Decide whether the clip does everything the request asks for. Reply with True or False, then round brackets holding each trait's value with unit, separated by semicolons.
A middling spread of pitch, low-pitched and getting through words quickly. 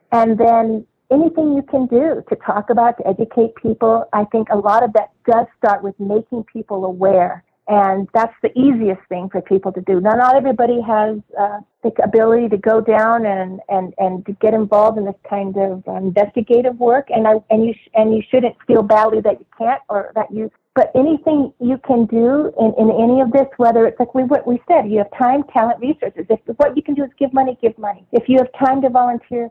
False (3.0 semitones; 225 Hz; 220 wpm)